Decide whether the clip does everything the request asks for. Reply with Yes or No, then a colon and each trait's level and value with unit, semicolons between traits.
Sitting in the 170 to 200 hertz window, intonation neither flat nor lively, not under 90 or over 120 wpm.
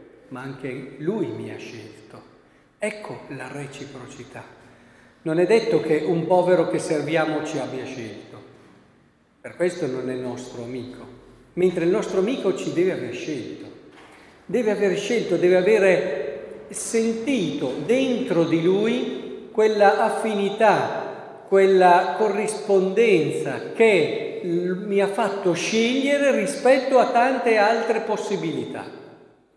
No: high, 190 Hz; wide, 6.5 semitones; slow, 115 wpm